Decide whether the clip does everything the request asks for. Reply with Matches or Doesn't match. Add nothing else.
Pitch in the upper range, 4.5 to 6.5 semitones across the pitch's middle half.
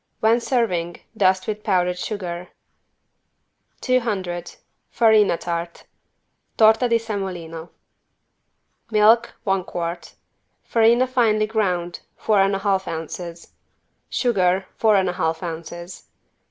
Doesn't match